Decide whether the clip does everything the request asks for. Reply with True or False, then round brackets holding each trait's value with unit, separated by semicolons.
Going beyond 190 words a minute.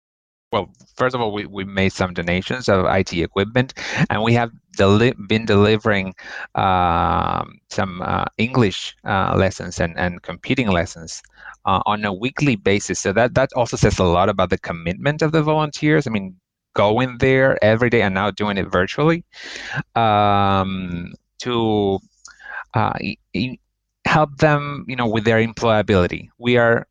False (155 wpm)